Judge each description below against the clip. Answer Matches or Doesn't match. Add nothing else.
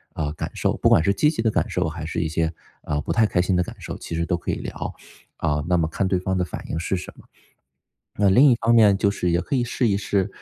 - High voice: Doesn't match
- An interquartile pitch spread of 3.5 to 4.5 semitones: Matches